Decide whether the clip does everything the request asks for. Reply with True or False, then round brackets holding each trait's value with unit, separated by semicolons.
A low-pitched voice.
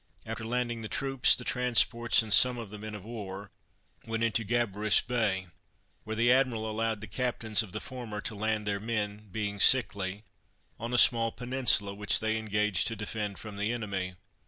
True (110 Hz)